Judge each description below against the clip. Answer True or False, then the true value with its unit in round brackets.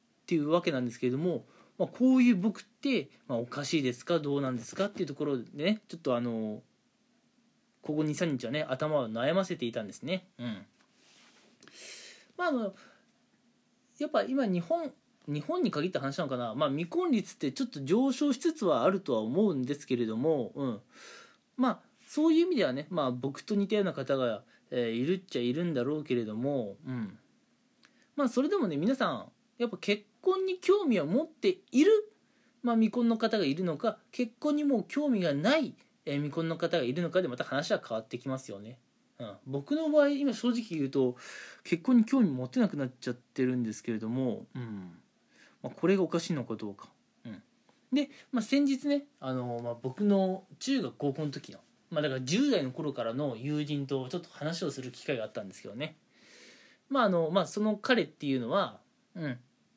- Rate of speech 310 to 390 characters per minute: True (365 characters per minute)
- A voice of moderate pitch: True (180 Hz)